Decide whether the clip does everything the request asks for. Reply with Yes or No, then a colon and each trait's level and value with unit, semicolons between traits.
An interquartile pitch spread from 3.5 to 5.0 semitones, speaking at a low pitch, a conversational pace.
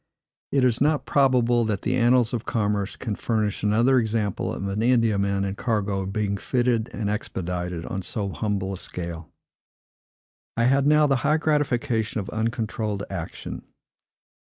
Yes: average, 3.8 semitones; low, 110 Hz; average, 150 wpm